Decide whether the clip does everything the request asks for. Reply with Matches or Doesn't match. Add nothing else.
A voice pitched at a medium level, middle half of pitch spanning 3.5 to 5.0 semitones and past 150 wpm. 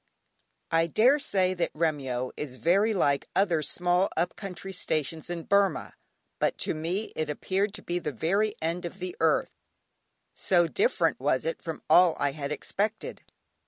Matches